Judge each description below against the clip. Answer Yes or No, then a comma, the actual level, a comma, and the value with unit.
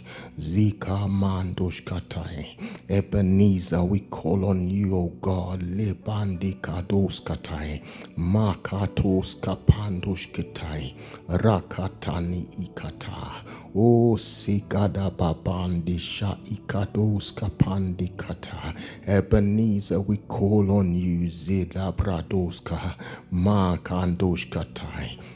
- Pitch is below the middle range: Yes, very low, 95 Hz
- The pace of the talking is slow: Yes, slow, 65 wpm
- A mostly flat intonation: Yes, narrow, 2.3 semitones